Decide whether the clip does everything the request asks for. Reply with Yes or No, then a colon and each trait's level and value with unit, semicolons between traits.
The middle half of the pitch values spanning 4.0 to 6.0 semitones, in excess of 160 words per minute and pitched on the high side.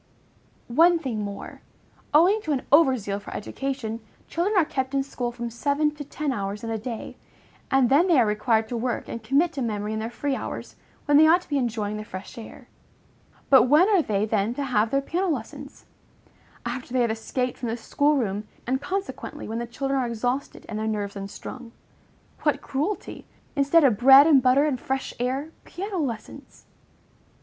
Yes: average, 4.6 semitones; average, 195 wpm; very high, 255 Hz